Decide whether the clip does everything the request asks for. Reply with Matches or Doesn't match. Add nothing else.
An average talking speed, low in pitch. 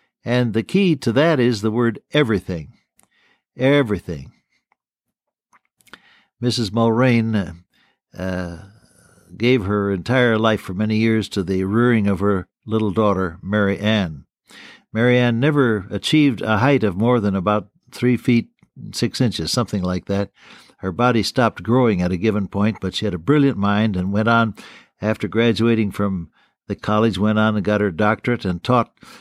Matches